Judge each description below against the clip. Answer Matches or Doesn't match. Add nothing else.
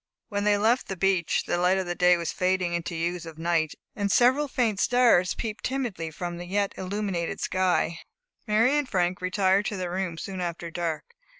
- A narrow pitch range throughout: Doesn't match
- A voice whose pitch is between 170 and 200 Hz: Matches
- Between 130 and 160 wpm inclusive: Doesn't match